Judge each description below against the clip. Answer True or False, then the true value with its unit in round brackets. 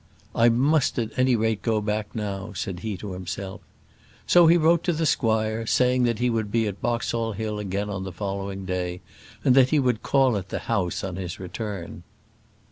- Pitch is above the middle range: False (110 Hz)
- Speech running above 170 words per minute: True (205 wpm)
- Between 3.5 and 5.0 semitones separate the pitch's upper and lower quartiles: True (3.9 semitones)